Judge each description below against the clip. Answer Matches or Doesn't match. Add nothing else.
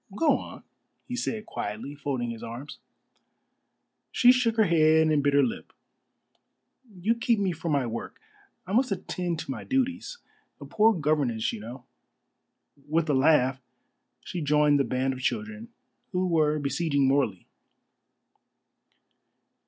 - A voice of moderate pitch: Matches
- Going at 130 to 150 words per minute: Matches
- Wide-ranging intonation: Matches